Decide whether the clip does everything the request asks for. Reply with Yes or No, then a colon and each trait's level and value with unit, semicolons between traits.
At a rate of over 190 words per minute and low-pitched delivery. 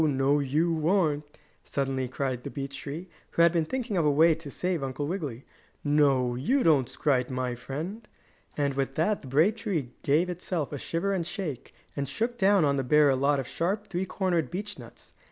No: average, 200 wpm; medium, 150 Hz